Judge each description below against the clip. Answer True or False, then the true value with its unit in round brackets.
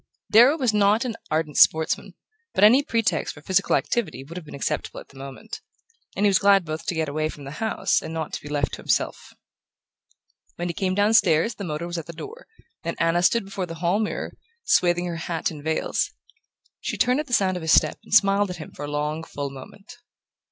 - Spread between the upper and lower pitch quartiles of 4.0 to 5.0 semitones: True (4.7 semitones)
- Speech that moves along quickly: True (220 wpm)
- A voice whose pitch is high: False (175 Hz)